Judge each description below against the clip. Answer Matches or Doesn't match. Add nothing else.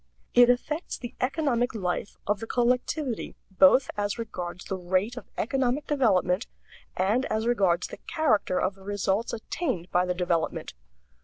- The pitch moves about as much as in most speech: Matches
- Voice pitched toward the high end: Matches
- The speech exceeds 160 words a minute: Doesn't match